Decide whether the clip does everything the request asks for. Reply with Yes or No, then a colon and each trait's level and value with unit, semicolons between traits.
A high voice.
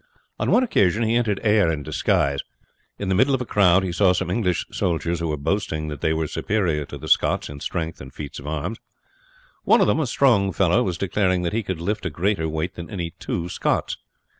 No: very low, 90 Hz